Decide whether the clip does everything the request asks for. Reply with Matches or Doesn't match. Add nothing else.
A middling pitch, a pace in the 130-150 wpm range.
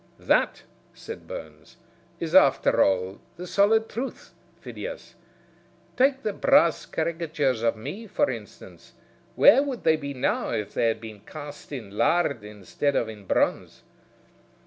Matches